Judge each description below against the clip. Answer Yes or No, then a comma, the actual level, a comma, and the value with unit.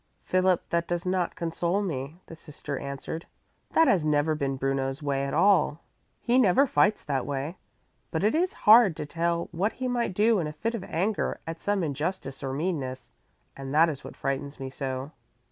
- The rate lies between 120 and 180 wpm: No, average, 190 wpm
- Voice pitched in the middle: Yes, medium, 165 Hz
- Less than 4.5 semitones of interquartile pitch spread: No, wide, 5.4 semitones